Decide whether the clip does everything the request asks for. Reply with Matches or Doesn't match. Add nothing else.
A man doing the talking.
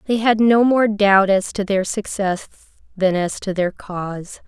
Doesn't match